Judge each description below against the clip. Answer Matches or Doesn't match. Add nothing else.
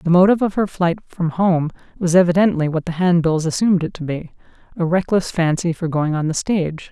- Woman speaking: Matches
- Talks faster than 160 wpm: Matches